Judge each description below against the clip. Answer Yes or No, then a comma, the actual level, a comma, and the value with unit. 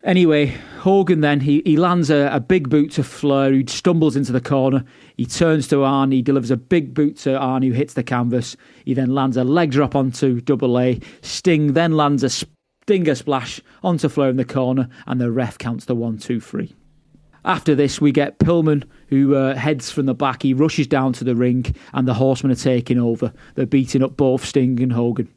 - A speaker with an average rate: No, fast, 215 wpm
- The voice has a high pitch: No, low, 135 Hz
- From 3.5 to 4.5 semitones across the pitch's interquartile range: No, average, 2.7 semitones